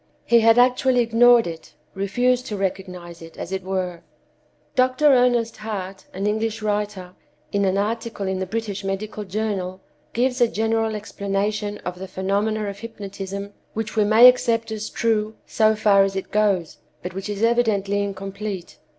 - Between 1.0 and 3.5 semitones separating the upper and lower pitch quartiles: Yes, average, 2.7 semitones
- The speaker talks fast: No, average, 160 wpm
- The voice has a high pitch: Yes, high, 210 Hz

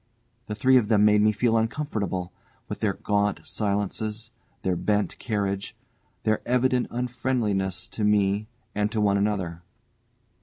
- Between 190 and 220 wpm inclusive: No, average, 140 wpm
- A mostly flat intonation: Yes, narrow, 2.2 semitones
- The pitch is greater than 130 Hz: No, low, 105 Hz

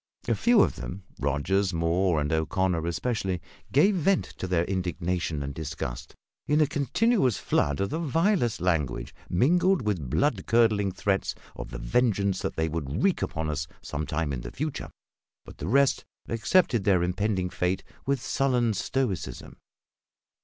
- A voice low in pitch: Yes, very low, 95 Hz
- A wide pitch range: Yes, wide, 7.8 semitones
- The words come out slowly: No, average, 155 wpm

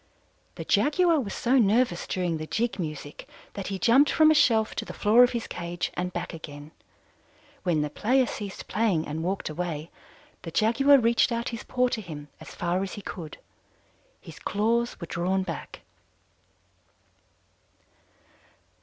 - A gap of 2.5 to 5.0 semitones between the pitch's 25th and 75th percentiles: No, wide, 5.6 semitones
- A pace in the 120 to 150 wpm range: No, average, 160 wpm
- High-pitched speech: Yes, high, 200 Hz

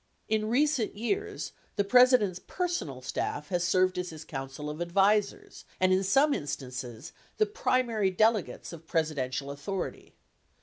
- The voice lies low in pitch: No, medium, 185 Hz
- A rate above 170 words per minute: No, average, 145 wpm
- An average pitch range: No, wide, 7.2 semitones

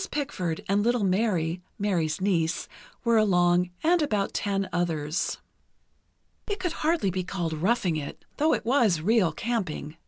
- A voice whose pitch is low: No, high, 195 Hz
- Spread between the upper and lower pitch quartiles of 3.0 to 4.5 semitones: No, wide, 5.5 semitones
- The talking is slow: No, average, 150 wpm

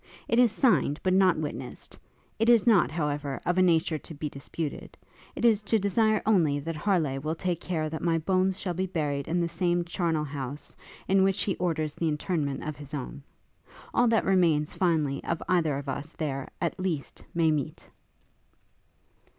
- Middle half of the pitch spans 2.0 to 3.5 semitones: No, average, 3.9 semitones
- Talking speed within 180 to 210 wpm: Yes, average, 185 wpm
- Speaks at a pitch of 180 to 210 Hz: No, medium, 165 Hz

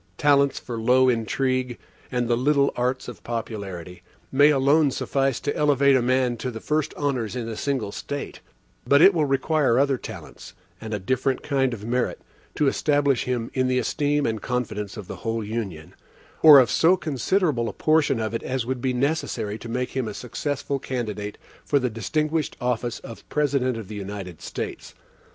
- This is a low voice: Yes, low, 125 Hz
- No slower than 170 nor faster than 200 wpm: Yes, average, 180 wpm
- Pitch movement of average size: Yes, average, 3.8 semitones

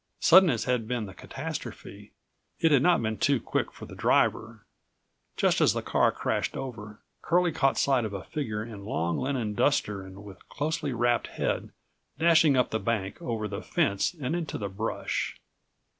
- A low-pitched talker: Yes, low, 120 Hz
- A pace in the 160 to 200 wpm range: Yes, average, 175 wpm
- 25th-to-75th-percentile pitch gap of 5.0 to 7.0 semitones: Yes, average, 5.3 semitones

